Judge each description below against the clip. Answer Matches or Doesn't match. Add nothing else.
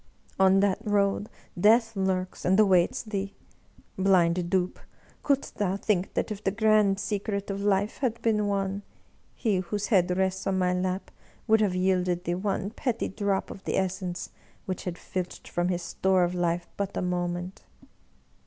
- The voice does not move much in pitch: Matches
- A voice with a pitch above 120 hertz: Matches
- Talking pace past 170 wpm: Doesn't match